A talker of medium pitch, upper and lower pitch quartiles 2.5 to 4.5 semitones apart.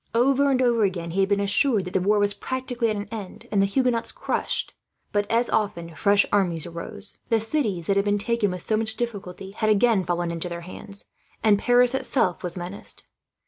No: high, 205 Hz; average, 4.0 semitones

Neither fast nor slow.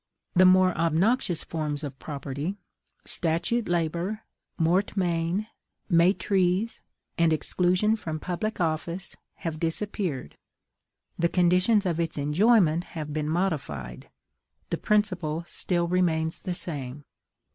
No: slow, 105 wpm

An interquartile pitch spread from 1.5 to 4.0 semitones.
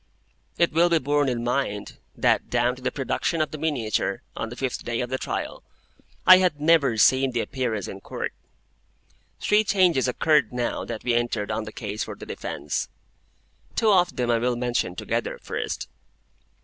No: average, 4.7 semitones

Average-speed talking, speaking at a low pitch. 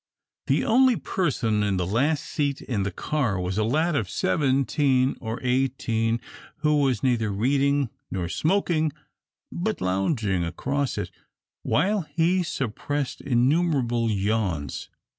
No: slow, 125 wpm; low, 130 Hz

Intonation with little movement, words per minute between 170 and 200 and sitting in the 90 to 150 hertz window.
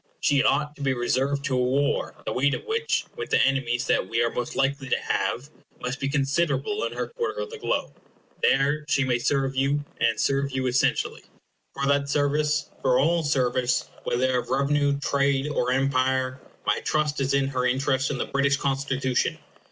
Yes: narrow, 1.7 semitones; average, 190 wpm; medium, 140 Hz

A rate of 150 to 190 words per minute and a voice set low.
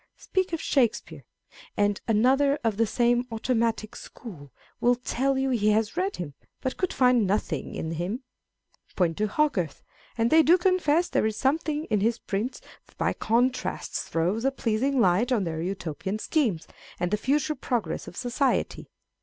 No: average, 170 wpm; high, 235 Hz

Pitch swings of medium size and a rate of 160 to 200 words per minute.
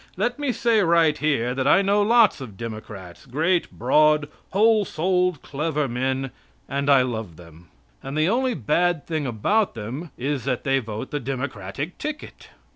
No: wide, 6.3 semitones; average, 165 wpm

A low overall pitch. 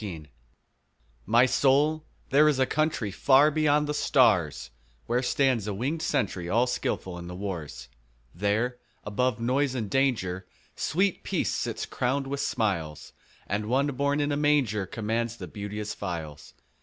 Yes: low, 120 Hz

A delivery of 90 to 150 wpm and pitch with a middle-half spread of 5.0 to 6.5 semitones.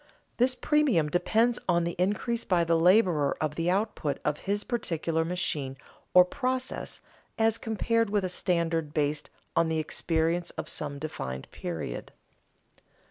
Yes: average, 140 wpm; wide, 5.6 semitones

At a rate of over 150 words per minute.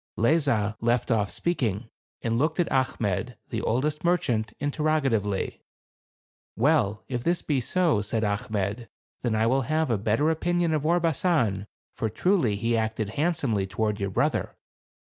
No: average, 140 wpm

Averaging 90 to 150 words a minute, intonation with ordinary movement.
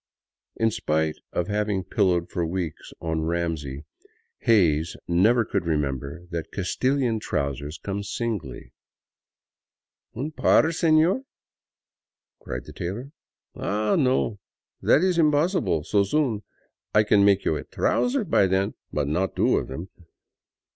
No: slow, 135 wpm; wide, 6.6 semitones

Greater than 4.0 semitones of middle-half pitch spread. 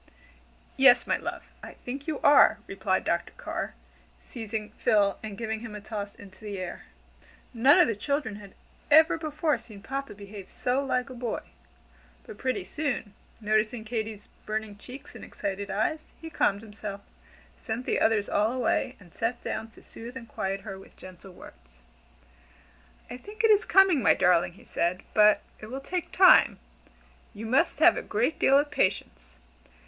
Yes: average, 5.2 semitones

